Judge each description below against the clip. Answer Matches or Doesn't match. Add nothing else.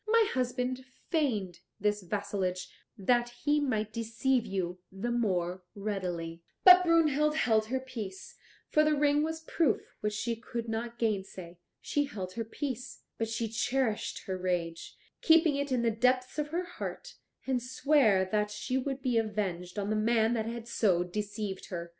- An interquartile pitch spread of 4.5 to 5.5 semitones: Matches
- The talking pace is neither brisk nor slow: Matches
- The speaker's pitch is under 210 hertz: Doesn't match